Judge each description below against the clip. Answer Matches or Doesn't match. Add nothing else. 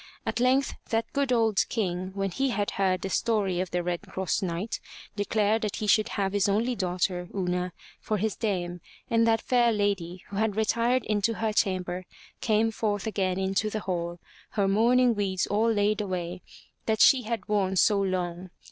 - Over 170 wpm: Matches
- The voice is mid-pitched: Doesn't match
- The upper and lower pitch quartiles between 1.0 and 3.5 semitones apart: Matches